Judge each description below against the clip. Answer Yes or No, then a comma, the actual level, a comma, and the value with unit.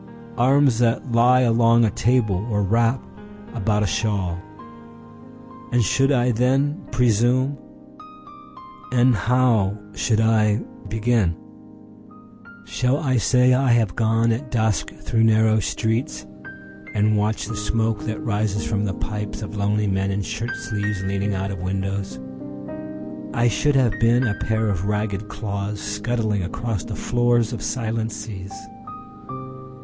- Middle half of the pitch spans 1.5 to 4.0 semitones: Yes, average, 2.8 semitones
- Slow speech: Yes, slow, 120 wpm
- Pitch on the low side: Yes, low, 110 Hz